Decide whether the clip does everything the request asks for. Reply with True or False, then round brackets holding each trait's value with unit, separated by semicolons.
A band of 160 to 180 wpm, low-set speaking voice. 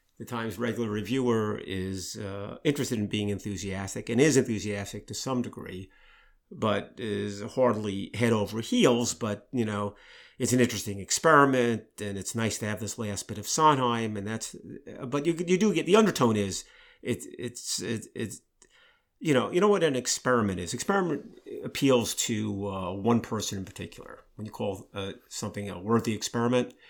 True (170 wpm; 110 Hz)